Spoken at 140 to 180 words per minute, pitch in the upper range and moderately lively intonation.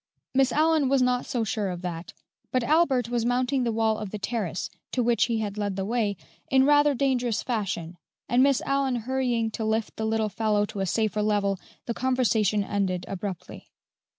No: average, 190 wpm; high, 225 Hz; average, 3.7 semitones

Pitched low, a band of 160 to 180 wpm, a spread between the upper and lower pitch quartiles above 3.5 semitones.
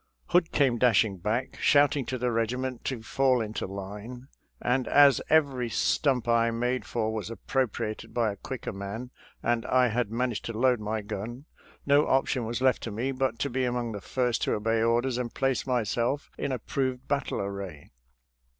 No: low, 120 Hz; average, 175 wpm; average, 2.8 semitones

